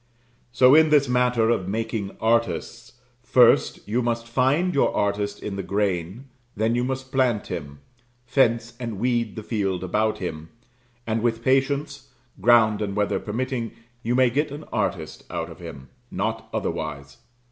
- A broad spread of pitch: No, average, 3.7 semitones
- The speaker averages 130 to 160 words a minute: Yes, average, 155 wpm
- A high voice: No, low, 115 Hz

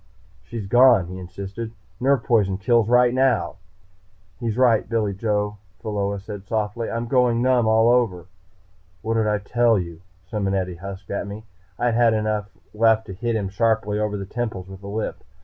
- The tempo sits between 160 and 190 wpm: Yes, average, 170 wpm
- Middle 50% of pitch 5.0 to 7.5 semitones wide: No, average, 2.8 semitones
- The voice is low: Yes, low, 110 Hz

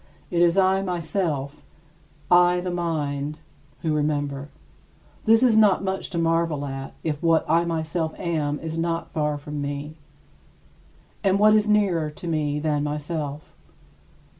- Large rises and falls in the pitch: No, average, 3.1 semitones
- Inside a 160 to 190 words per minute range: No, average, 140 wpm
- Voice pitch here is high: No, medium, 160 Hz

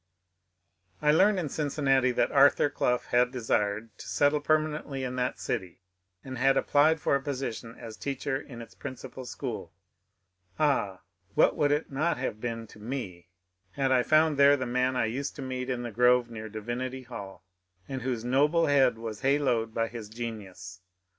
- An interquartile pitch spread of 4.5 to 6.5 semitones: No, average, 3.6 semitones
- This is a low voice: Yes, low, 130 Hz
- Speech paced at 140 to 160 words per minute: No, average, 175 wpm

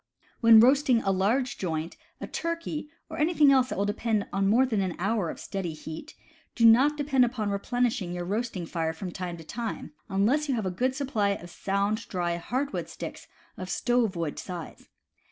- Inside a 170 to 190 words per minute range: Yes, average, 185 wpm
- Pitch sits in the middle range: No, high, 215 Hz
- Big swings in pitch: Yes, wide, 5.7 semitones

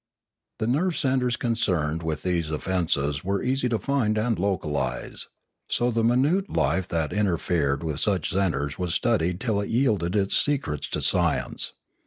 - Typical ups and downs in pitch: No, wide, 6.7 semitones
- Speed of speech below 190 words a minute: Yes, average, 160 wpm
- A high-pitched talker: No, low, 100 Hz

